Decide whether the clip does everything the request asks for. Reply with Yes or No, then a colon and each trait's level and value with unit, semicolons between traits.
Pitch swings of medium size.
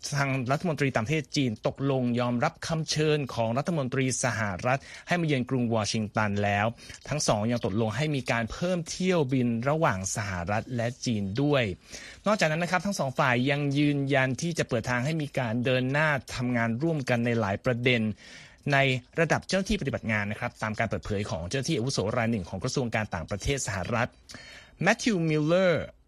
Yes: average, 4.8 semitones